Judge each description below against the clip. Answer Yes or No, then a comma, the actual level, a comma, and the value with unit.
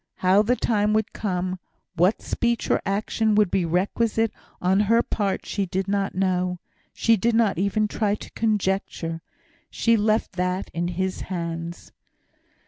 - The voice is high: Yes, high, 195 Hz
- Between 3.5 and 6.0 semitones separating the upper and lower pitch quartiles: No, average, 2.9 semitones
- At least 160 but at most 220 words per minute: No, average, 150 wpm